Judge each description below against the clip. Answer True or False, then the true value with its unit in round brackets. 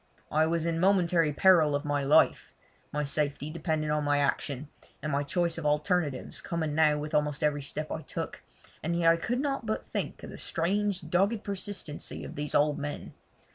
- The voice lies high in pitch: False (155 Hz)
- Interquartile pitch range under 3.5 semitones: True (2.8 semitones)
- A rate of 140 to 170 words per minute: False (190 wpm)